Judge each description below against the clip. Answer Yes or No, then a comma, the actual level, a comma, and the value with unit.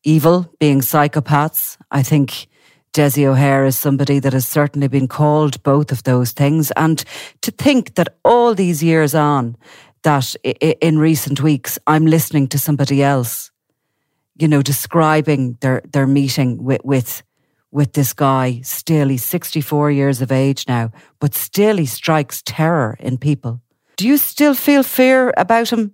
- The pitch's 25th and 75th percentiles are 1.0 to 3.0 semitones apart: Yes, average, 2.7 semitones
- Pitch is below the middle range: No, medium, 145 Hz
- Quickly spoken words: No, average, 155 wpm